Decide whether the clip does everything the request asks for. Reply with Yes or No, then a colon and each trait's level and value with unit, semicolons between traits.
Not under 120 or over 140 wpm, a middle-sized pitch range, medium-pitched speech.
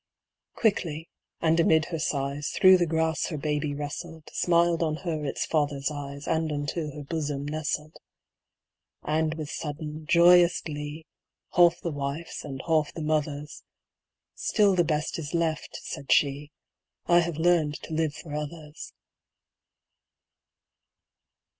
No: slow, 135 wpm; narrow, 2.2 semitones; medium, 155 Hz